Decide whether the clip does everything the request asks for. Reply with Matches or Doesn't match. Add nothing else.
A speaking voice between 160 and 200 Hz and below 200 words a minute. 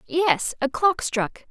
Doesn't match